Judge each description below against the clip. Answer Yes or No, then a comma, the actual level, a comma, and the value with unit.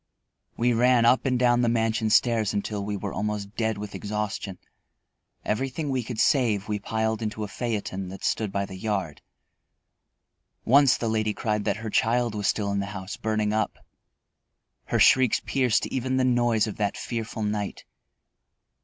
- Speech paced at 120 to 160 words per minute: No, average, 170 wpm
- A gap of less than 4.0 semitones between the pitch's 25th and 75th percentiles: Yes, narrow, 2.6 semitones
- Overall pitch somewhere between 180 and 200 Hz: No, low, 110 Hz